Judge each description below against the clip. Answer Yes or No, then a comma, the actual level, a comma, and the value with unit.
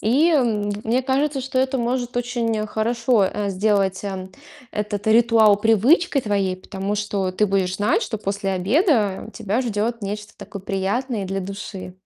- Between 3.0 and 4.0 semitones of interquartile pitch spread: Yes, average, 3.5 semitones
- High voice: Yes, high, 210 Hz